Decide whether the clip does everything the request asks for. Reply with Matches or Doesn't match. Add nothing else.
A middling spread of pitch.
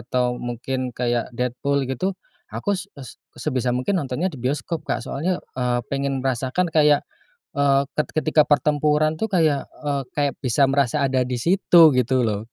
Matches